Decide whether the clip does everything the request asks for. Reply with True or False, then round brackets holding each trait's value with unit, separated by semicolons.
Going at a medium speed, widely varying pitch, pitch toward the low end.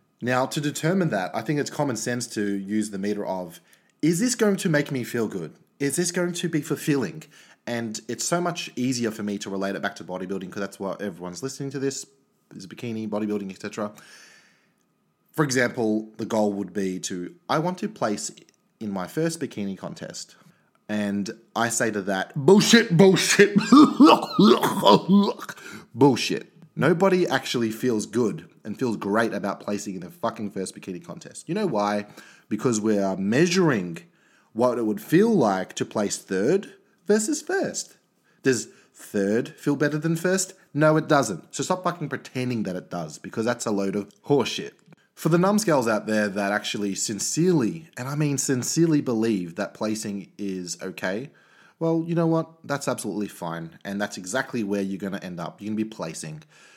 True (180 wpm; 8.2 semitones; 120 Hz)